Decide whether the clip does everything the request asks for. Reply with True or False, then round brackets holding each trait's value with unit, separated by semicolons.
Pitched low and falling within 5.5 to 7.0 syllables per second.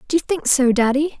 False (280 Hz; 6.2 syllables/s)